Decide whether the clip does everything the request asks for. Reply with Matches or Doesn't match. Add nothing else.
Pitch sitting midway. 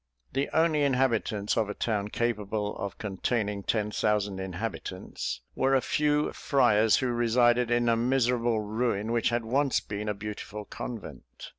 Doesn't match